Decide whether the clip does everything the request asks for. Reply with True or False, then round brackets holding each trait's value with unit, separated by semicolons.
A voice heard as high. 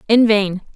True (210 Hz)